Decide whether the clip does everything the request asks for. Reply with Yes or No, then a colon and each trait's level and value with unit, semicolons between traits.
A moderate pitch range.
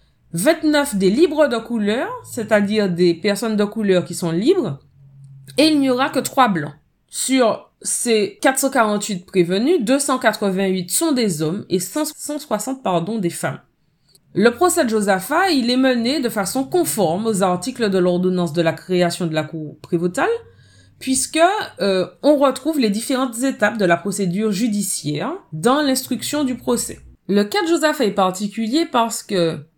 No: wide, 6.6 semitones